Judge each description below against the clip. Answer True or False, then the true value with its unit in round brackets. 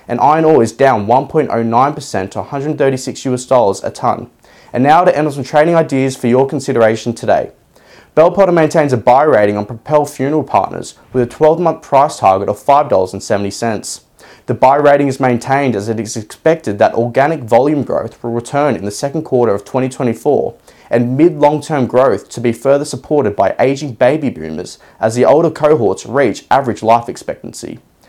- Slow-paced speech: False (175 wpm)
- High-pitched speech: False (130 Hz)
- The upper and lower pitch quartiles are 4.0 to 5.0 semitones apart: True (4.3 semitones)